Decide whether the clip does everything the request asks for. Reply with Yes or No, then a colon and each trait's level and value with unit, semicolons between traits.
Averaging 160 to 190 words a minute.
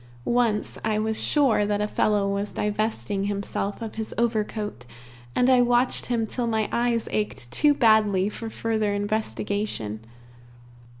No: average, 140 wpm